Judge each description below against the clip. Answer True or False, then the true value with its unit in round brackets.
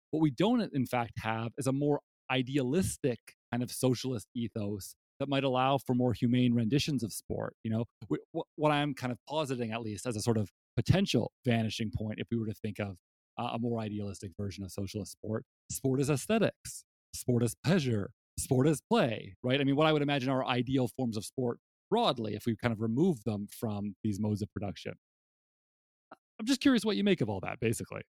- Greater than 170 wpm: True (205 wpm)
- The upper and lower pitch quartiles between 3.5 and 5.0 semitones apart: True (4.2 semitones)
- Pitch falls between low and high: False (120 Hz)